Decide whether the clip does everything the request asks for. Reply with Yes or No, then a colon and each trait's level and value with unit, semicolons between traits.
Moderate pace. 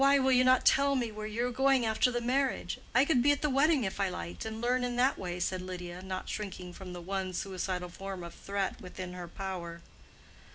No: fast, 235 wpm